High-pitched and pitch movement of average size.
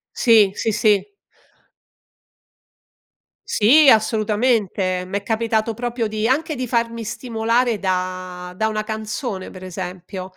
Yes: high, 220 Hz; average, 3.6 semitones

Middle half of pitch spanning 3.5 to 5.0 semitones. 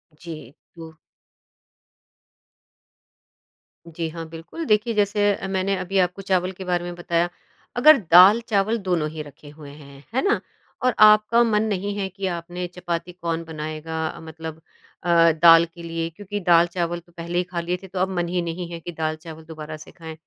No: average, 2.9 semitones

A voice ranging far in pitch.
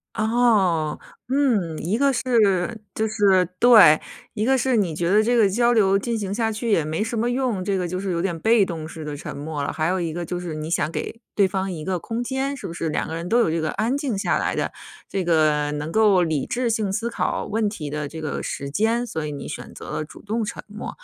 Yes: wide, 5.8 semitones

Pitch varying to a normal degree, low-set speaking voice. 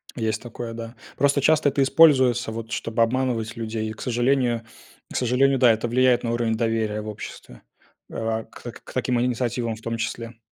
No: narrow, 2.1 semitones; low, 115 Hz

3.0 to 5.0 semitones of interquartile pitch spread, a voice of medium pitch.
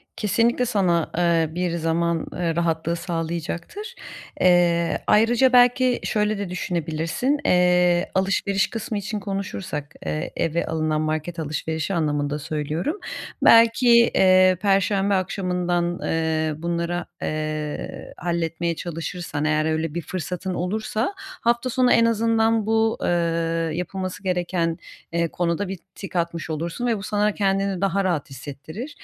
Yes: average, 3.8 semitones; medium, 175 Hz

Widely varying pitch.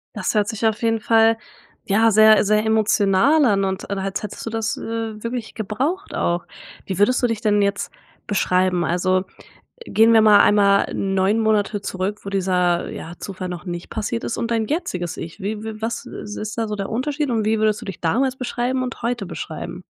No: narrow, 2.6 semitones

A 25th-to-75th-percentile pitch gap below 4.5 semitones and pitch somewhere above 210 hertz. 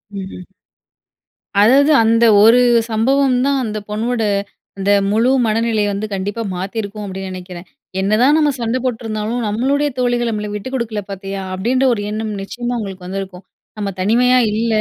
Yes: average, 3.6 semitones; high, 220 Hz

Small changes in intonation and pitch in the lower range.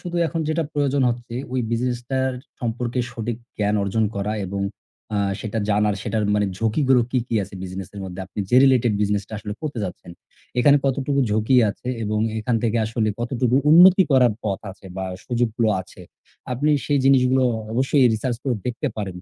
No: average, 3.8 semitones; low, 120 Hz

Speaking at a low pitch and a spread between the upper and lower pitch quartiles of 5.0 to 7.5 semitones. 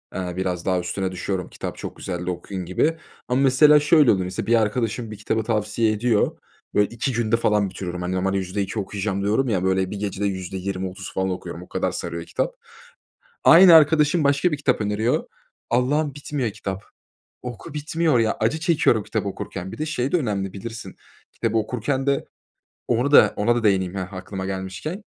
Yes: low, 105 Hz; wide, 5.6 semitones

